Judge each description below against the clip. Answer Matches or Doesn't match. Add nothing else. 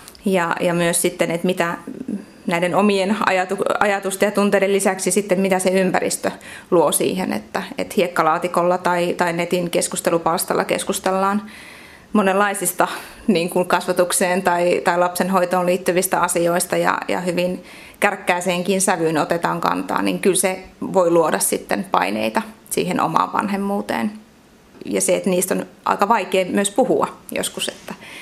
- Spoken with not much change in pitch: Matches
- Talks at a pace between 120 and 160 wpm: Matches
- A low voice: Doesn't match